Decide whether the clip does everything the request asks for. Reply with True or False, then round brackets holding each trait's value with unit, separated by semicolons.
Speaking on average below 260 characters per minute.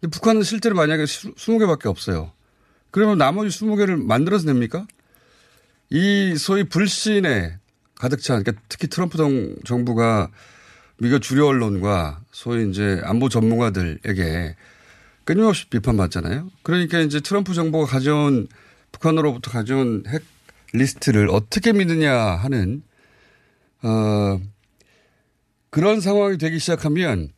False (280 characters per minute)